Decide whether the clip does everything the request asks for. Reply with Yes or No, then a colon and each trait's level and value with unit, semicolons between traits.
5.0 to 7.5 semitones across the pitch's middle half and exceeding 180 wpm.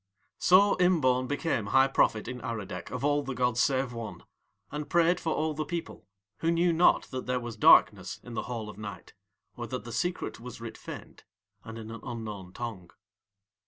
Yes: average, 5.3 semitones; average, 190 wpm